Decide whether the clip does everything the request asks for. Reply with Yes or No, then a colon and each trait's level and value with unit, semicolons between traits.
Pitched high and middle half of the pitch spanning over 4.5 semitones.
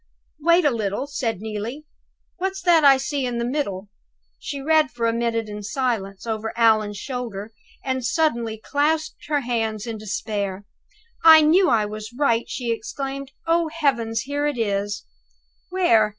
Yes: high, 235 Hz; average, 5.0 semitones